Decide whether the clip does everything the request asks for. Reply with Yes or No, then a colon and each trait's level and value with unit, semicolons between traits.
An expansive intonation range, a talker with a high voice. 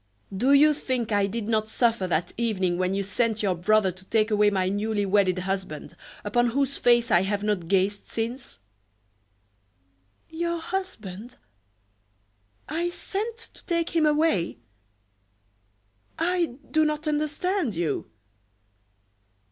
Yes: wide, 7.6 semitones; high, 220 Hz